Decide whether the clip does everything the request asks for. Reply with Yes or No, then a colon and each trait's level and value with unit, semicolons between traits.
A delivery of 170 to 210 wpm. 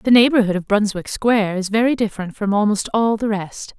Yes: fast, 205 wpm